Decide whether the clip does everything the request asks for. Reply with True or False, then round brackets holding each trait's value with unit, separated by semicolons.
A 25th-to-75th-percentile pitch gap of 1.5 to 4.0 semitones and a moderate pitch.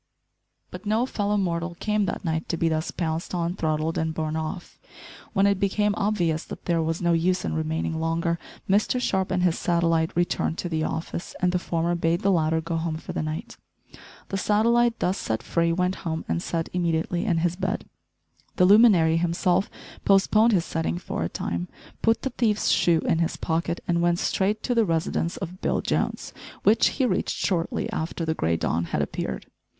True (3.2 semitones; 170 Hz)